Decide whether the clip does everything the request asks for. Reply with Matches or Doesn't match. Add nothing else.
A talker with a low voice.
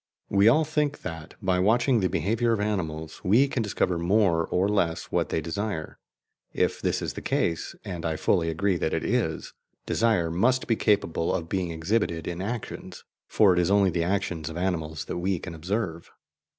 Matches